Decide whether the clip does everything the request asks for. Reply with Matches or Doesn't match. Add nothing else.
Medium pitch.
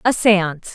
Doesn't match